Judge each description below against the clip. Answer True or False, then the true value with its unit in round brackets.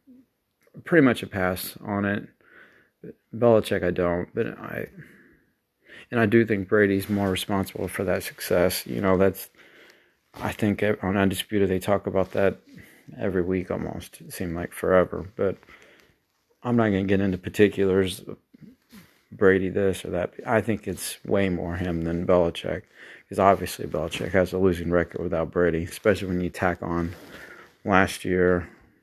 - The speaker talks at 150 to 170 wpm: True (155 wpm)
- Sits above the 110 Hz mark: False (95 Hz)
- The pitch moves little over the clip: True (2.2 semitones)